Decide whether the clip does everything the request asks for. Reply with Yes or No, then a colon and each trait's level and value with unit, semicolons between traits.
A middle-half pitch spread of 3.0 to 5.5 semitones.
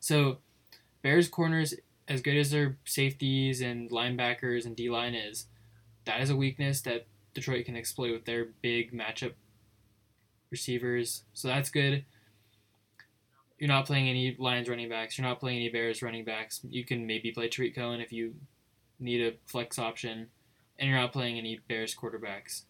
No: narrow, 2.6 semitones